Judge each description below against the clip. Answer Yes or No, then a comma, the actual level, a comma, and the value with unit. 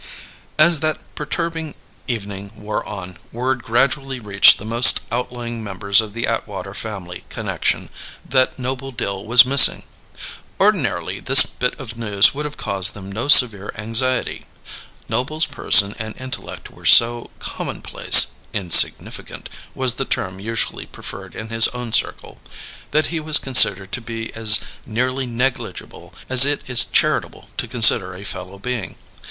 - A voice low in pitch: Yes, low, 115 Hz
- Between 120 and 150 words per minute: Yes, average, 145 wpm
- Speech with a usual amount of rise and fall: Yes, average, 4.0 semitones